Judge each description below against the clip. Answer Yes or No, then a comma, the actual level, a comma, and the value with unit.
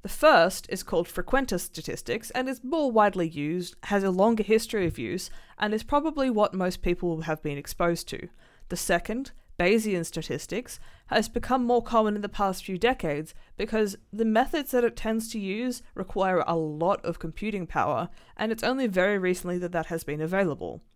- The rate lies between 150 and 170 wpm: No, average, 185 wpm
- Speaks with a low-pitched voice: No, high, 195 Hz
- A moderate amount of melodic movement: Yes, average, 4.5 semitones